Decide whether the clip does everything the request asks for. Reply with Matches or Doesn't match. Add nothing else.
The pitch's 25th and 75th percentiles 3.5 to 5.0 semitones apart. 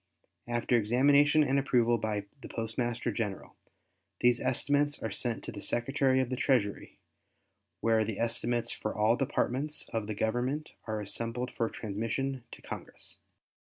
Doesn't match